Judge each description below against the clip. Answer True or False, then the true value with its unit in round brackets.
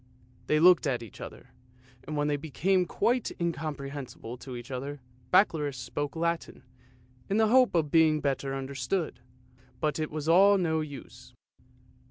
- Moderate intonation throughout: True (3.6 semitones)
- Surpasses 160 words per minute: False (155 wpm)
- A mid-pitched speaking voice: True (155 Hz)